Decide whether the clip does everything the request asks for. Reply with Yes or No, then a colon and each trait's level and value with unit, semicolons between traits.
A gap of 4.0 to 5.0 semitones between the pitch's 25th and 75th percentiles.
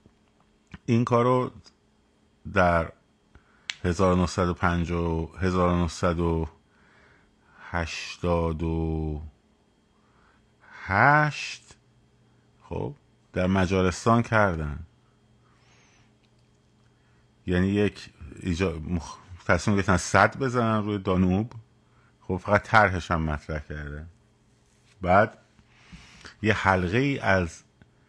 Yes: average, 4.3 semitones